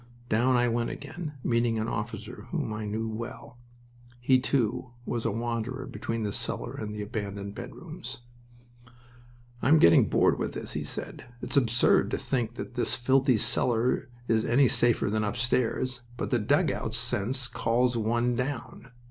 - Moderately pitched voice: No, low, 120 Hz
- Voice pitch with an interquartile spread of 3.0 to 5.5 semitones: No, narrow, 2.5 semitones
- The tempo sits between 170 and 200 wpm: No, average, 160 wpm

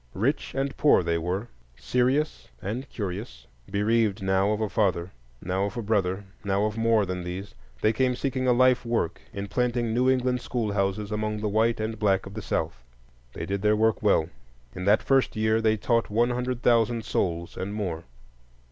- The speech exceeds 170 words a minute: Yes, average, 185 wpm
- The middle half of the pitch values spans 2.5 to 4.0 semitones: Yes, average, 3.5 semitones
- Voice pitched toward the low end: Yes, low, 110 Hz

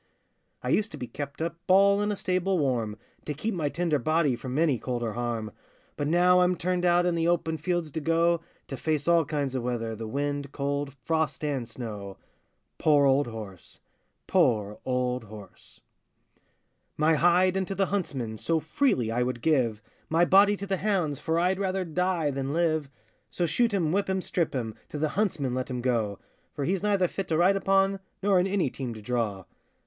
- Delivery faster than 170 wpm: Yes, average, 195 wpm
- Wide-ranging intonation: Yes, wide, 6.2 semitones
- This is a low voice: No, medium, 155 Hz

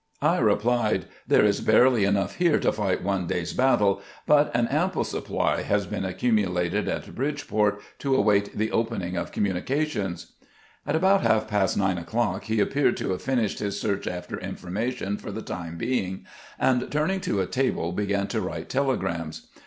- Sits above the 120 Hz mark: No, low, 105 Hz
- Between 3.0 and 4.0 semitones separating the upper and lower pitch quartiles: No, average, 5.0 semitones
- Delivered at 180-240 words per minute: No, average, 170 wpm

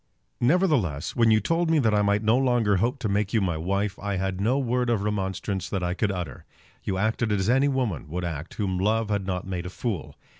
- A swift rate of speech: Yes, fast, 230 wpm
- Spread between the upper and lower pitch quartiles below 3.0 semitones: No, average, 3.9 semitones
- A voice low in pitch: Yes, low, 105 Hz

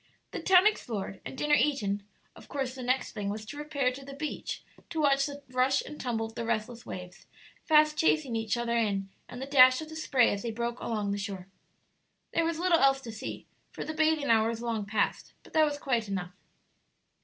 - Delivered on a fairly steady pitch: No, average, 5.0 semitones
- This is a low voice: No, very high, 255 Hz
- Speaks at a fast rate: Yes, fast, 215 wpm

